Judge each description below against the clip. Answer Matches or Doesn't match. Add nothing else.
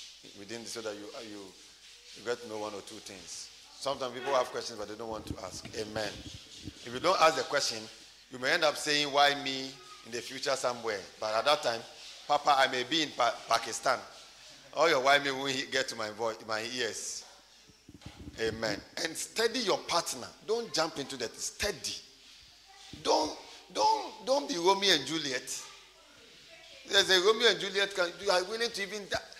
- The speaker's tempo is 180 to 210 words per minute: Matches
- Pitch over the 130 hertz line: Matches